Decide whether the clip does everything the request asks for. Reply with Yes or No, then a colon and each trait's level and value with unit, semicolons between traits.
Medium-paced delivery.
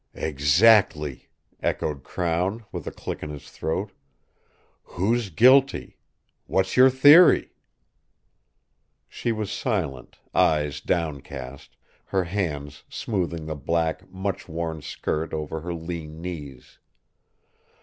No: slow, 105 wpm